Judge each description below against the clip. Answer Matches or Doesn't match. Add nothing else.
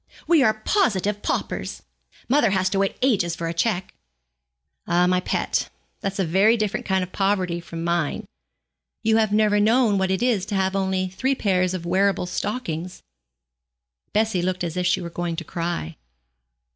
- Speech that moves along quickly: Doesn't match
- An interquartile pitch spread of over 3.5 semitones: Doesn't match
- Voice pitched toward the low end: Doesn't match